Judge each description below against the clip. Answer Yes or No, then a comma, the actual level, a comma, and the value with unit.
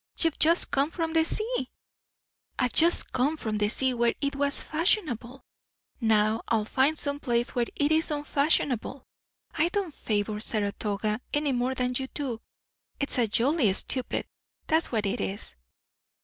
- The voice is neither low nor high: No, very high, 260 Hz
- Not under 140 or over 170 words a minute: Yes, average, 155 wpm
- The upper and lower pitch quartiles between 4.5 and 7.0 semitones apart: Yes, average, 5.3 semitones